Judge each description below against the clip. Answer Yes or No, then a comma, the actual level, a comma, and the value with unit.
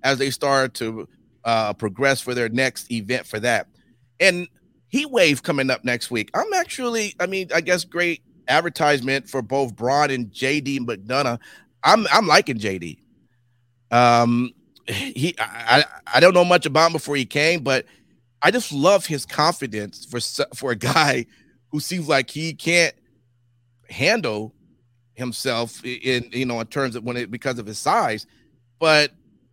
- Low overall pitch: Yes, low, 130 Hz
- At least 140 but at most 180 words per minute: Yes, average, 165 wpm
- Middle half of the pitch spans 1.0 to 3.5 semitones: No, average, 4.1 semitones